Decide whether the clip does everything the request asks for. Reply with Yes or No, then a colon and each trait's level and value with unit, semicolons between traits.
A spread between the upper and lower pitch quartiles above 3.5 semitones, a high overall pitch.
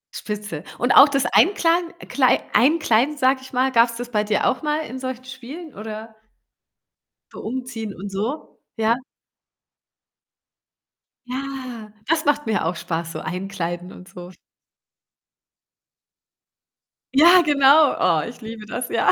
Yes: average, 4.6 semitones; high, 245 Hz